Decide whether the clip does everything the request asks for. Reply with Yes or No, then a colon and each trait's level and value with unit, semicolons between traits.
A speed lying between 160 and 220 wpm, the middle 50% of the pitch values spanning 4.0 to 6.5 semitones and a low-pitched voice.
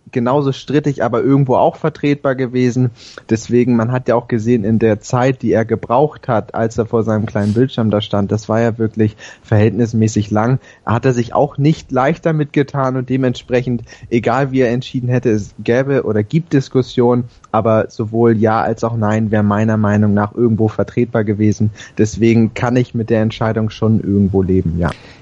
No: average, 185 wpm; average, 2.7 semitones; low, 115 Hz